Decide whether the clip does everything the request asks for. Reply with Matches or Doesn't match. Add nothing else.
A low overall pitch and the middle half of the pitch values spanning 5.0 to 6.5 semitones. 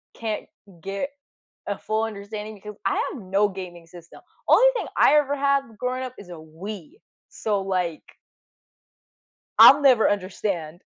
Doesn't match